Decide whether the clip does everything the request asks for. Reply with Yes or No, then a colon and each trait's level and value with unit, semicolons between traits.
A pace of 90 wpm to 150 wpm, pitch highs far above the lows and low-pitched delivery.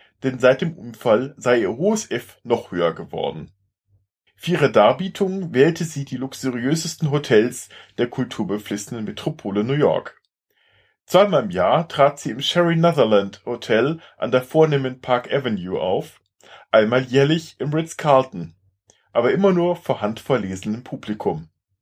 Yes: average, 135 wpm; wide, 6.9 semitones; low, 130 Hz